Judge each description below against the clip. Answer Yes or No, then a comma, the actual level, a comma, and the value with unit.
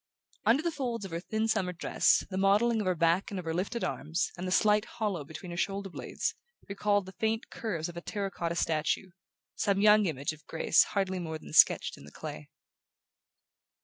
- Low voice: No, high, 190 Hz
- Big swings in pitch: No, average, 3.8 semitones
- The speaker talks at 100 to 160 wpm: No, fast, 205 wpm